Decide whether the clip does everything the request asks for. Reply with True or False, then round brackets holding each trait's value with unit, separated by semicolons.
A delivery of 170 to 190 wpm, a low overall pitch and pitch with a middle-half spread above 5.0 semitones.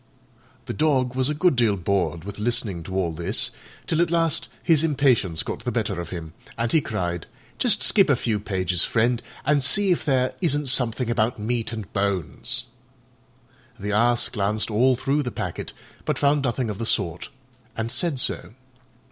True (180 wpm; 115 Hz; 5.5 semitones)